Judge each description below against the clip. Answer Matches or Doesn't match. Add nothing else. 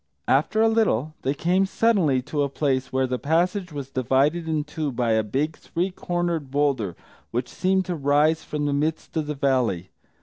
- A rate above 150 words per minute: Matches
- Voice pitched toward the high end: Doesn't match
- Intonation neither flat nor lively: Matches